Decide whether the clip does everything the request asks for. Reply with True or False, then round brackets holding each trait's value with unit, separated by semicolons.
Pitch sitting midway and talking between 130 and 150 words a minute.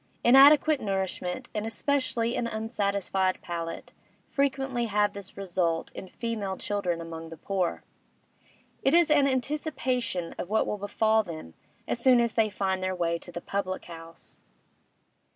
False (205 Hz; 145 wpm)